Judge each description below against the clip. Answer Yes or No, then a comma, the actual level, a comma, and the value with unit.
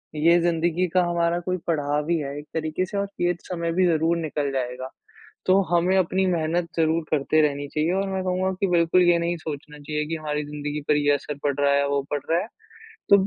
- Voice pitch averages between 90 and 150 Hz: No, medium, 160 Hz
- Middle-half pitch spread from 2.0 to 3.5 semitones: Yes, average, 2.9 semitones